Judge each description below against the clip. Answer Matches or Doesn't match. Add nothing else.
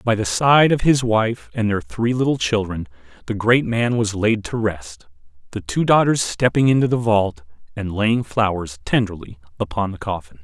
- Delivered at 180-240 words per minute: Matches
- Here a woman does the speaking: Doesn't match